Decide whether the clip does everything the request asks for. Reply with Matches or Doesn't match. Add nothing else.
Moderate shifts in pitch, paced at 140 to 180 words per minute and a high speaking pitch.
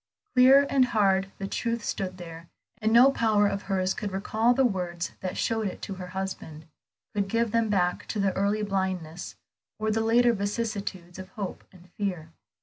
Matches